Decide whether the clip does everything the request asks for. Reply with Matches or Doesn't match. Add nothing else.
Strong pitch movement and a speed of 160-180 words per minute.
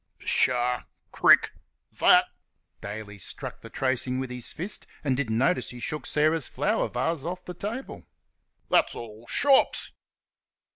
Doesn't match